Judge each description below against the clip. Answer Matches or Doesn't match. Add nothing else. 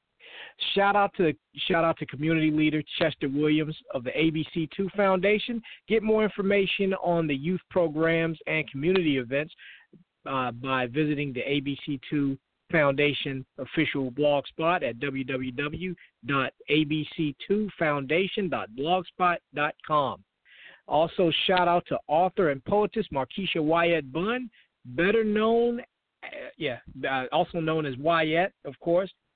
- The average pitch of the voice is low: Doesn't match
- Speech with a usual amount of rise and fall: Matches